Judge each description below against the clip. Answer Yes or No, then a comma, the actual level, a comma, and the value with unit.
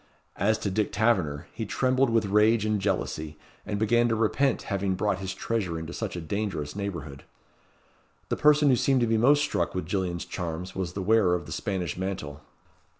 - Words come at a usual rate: Yes, average, 190 wpm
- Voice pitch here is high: No, low, 100 Hz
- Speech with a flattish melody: No, average, 4.2 semitones